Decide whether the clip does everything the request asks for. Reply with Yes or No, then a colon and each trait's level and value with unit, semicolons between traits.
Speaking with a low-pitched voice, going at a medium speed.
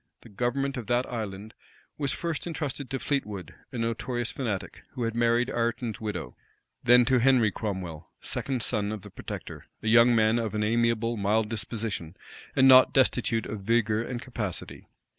Yes: low, 115 Hz; average, 165 wpm